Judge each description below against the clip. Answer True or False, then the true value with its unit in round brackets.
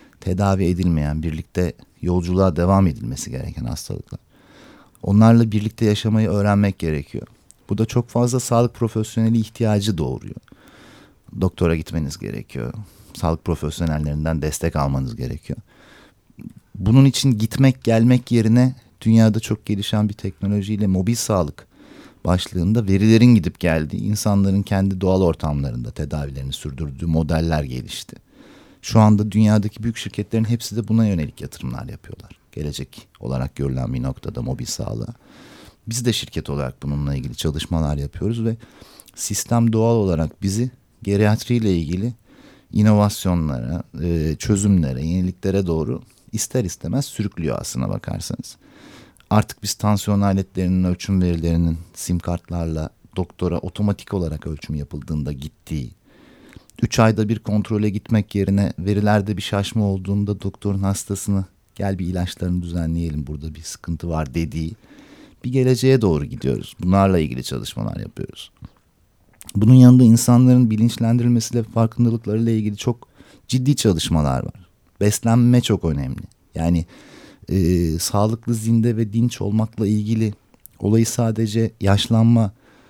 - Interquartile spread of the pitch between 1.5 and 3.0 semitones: False (5.1 semitones)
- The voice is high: False (100 Hz)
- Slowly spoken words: False (115 wpm)